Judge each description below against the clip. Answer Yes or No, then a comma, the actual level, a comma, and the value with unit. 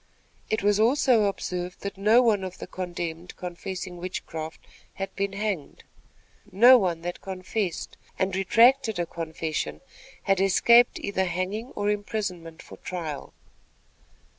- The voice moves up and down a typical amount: Yes, average, 3.0 semitones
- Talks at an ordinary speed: No, slow, 130 wpm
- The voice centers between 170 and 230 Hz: Yes, high, 190 Hz